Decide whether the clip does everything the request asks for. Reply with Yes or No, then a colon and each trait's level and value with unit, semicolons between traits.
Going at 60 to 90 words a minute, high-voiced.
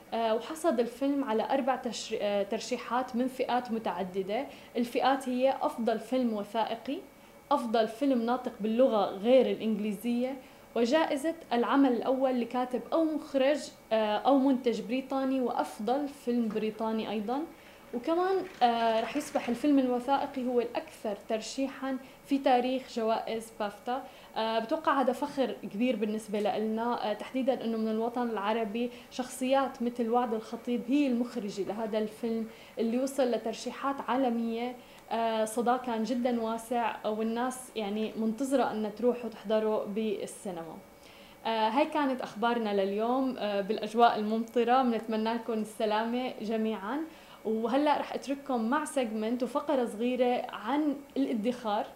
No: average, 110 wpm; high, 240 Hz